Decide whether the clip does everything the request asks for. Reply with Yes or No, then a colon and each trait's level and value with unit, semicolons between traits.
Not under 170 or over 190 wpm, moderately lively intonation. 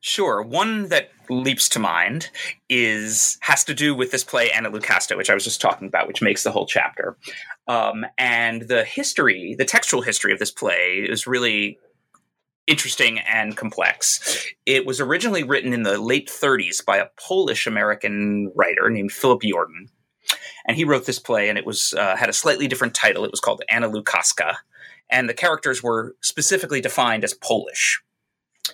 Yes: average, 175 wpm; average, 4.7 semitones